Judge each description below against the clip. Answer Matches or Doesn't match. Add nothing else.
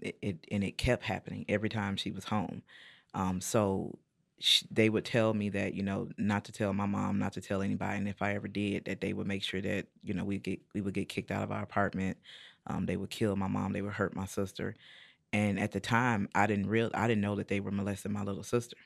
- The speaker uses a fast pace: Matches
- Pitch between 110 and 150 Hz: Doesn't match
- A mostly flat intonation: Matches